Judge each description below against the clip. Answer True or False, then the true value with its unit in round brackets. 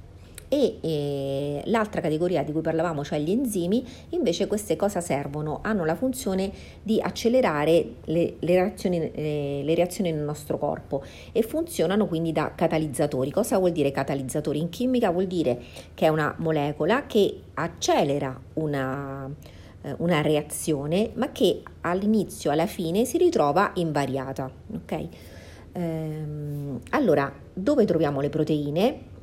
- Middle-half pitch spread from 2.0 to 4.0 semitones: False (5.0 semitones)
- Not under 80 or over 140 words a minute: True (135 wpm)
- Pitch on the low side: False (160 Hz)